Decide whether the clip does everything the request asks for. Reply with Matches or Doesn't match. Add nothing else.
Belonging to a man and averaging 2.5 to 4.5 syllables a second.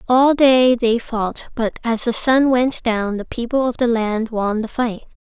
Doesn't match